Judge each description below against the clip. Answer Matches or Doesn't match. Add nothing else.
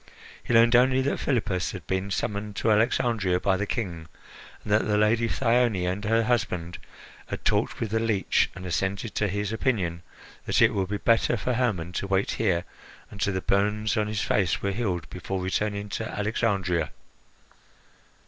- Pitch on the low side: Matches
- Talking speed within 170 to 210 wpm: Matches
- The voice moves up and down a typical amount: Matches